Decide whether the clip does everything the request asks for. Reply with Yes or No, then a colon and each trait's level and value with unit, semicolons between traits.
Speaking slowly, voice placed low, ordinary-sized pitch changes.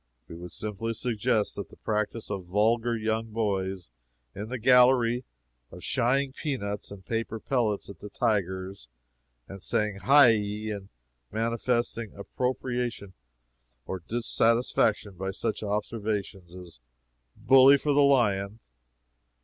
Yes: slow, 125 wpm; low, 110 Hz; average, 3.3 semitones